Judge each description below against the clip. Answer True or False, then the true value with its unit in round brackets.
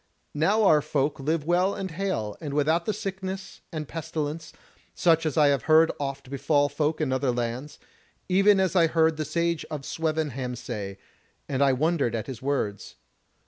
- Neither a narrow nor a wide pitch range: True (3.5 semitones)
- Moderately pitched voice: True (155 Hz)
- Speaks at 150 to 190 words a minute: True (175 wpm)